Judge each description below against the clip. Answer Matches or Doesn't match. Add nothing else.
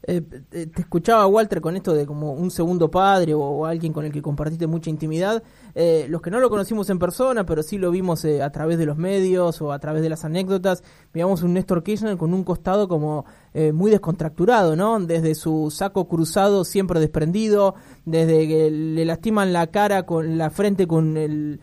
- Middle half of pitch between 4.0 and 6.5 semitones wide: Doesn't match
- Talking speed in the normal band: Doesn't match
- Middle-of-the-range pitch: Matches